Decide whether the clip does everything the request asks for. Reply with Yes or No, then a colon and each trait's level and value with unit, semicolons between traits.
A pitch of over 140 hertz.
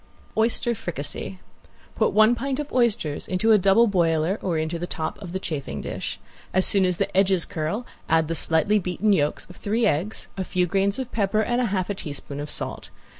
Yes: high, 190 Hz